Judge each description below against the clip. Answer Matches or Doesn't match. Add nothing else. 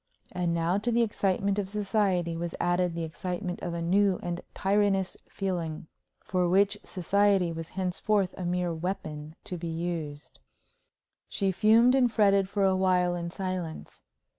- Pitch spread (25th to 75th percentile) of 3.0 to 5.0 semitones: Doesn't match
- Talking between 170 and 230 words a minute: Doesn't match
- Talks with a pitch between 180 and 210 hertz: Matches